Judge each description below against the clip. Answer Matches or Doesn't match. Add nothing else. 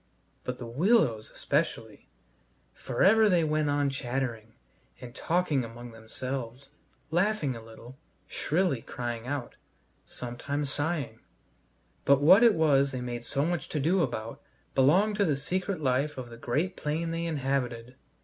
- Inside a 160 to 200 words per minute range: Doesn't match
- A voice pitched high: Doesn't match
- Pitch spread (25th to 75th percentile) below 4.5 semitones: Doesn't match